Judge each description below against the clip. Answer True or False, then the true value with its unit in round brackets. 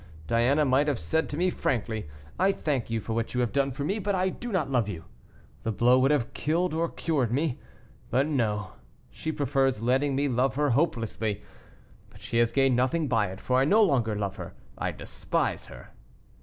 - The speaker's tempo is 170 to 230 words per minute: True (205 wpm)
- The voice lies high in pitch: False (135 Hz)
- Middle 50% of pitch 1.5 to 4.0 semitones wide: False (4.5 semitones)